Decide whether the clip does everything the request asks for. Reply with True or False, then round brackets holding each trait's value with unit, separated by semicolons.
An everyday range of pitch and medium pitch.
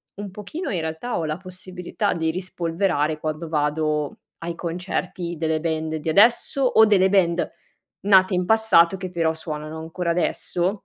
True (3.0 semitones; 170 Hz)